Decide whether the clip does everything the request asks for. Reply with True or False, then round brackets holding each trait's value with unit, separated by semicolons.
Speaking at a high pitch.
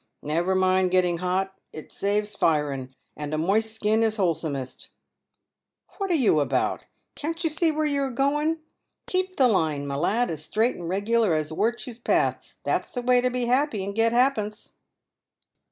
True (210 Hz)